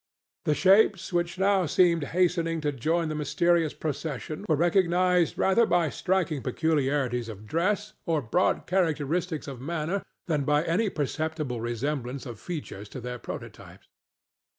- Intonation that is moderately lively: Yes, average, 4.0 semitones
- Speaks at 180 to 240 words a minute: No, average, 140 wpm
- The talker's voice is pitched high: No, medium, 160 Hz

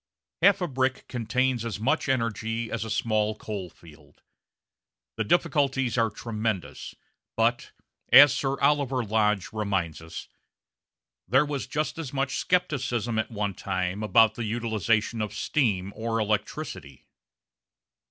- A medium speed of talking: No, slow, 130 wpm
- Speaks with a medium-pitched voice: No, low, 115 Hz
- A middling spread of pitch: Yes, average, 3.9 semitones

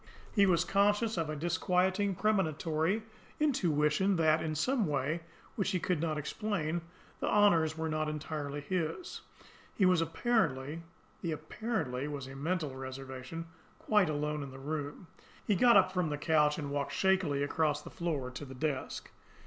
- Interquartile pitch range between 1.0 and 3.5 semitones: No, average, 4.3 semitones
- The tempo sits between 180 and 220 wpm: No, average, 160 wpm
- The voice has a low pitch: No, medium, 160 Hz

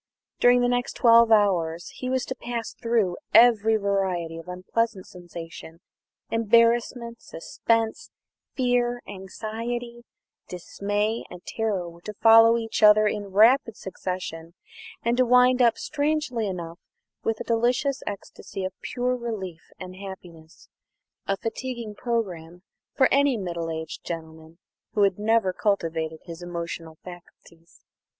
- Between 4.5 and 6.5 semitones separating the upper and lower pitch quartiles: Yes, average, 4.9 semitones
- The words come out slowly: Yes, slow, 130 wpm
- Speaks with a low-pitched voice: No, high, 210 Hz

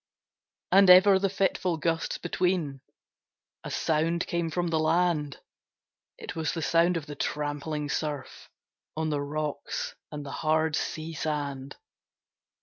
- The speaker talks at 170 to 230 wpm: No, slow, 135 wpm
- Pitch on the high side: No, medium, 160 Hz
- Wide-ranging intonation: No, narrow, 2.6 semitones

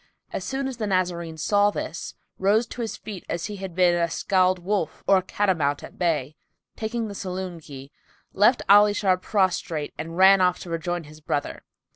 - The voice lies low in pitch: No, medium, 185 Hz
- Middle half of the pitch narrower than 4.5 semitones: Yes, average, 3.5 semitones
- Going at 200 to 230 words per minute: Yes, fast, 205 wpm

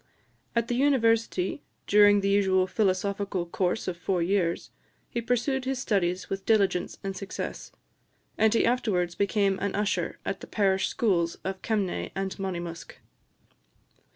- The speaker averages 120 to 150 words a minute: Yes, average, 140 wpm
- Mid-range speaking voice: No, high, 195 Hz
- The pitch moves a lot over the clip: No, average, 3.0 semitones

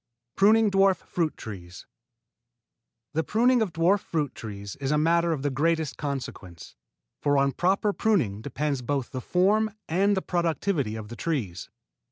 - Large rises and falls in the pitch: Yes, wide, 6.8 semitones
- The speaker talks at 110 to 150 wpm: No, average, 160 wpm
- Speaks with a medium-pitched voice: Yes, medium, 155 Hz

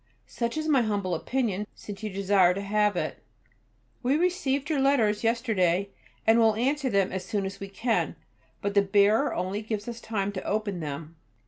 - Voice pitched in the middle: No, high, 210 Hz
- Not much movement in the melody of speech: No, average, 3.2 semitones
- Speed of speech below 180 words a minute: No, average, 185 wpm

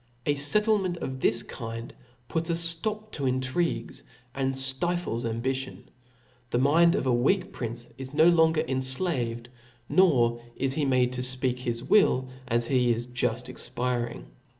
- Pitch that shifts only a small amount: No, average, 5.0 semitones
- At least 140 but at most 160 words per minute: Yes, average, 150 wpm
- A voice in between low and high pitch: No, low, 130 Hz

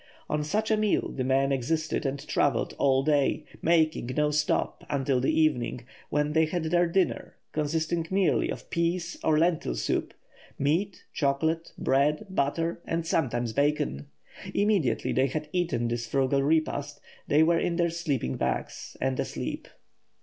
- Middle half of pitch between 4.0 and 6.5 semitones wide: No, average, 3.5 semitones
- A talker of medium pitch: Yes, medium, 150 Hz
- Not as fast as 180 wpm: Yes, average, 150 wpm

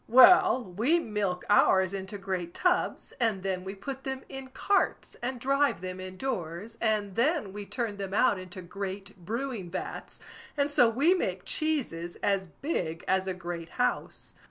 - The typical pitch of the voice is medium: No, high, 205 Hz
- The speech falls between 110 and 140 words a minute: No, average, 165 wpm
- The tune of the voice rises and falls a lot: Yes, wide, 5.8 semitones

